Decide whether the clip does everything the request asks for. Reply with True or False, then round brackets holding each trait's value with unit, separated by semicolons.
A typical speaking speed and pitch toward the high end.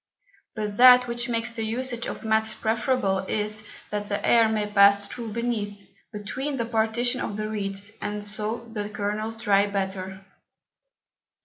True (150 wpm; 215 Hz)